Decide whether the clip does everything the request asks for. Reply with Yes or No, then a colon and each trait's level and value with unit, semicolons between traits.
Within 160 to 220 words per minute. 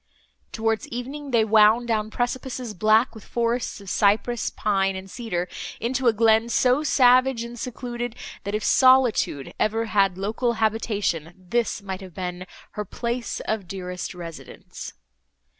No: average, 140 wpm